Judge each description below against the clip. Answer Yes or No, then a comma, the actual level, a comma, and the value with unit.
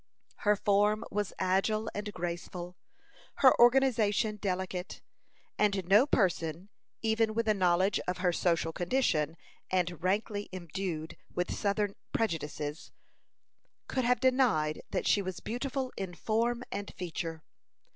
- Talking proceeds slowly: Yes, slow, 125 wpm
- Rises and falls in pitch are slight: No, average, 3.7 semitones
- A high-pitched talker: Yes, high, 195 Hz